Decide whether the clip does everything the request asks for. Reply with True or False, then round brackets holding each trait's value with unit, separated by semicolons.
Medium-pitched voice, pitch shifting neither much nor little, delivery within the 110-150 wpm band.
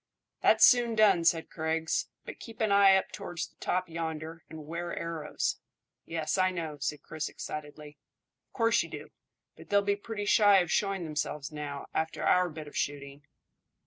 False (165 Hz; 4.4 semitones; 175 wpm)